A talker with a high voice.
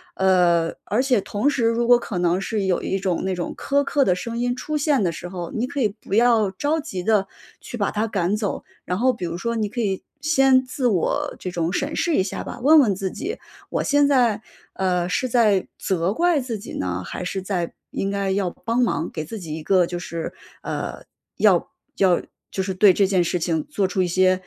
Yes: high, 200 Hz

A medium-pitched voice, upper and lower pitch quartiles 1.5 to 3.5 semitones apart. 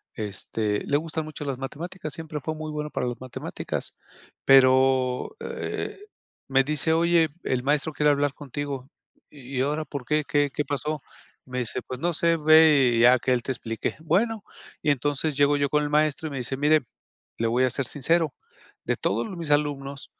Yes: medium, 145 Hz; average, 2.9 semitones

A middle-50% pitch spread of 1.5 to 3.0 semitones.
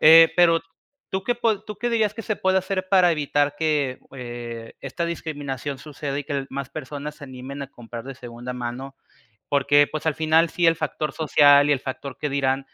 No: average, 3.7 semitones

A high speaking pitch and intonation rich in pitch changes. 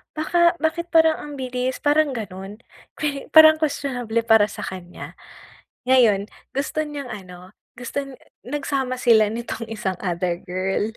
Yes: very high, 250 Hz; wide, 6.0 semitones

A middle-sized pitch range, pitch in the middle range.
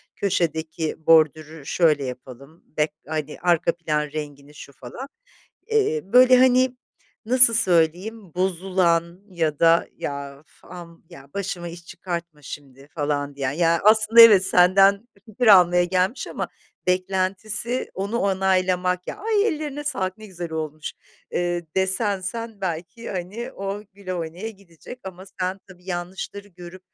Yes: average, 3.8 semitones; medium, 180 Hz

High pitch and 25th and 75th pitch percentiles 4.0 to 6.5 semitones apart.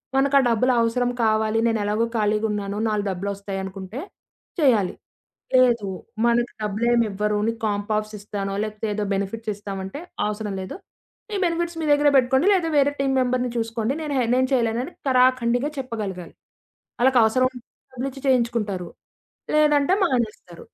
No: high, 230 Hz; average, 3.6 semitones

